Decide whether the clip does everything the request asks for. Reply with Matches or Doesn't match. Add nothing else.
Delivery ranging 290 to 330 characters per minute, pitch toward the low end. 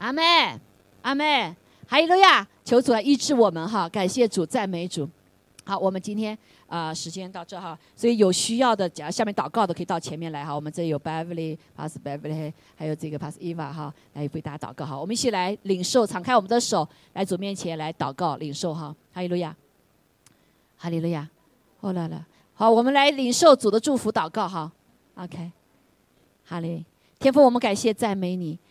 Doesn't match